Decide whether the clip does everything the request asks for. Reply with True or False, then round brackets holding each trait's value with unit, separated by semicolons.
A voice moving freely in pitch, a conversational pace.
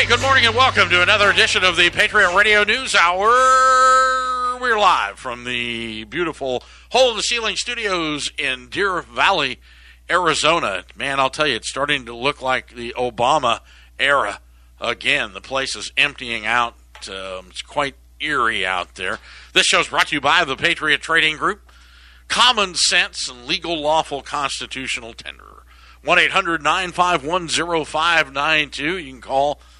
True (7.8 semitones; 165 wpm)